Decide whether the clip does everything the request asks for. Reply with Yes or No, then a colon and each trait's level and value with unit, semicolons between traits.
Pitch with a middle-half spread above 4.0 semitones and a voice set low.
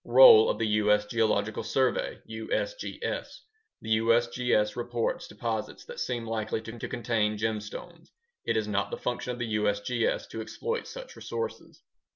No: narrow, 2.5 semitones; low, 115 Hz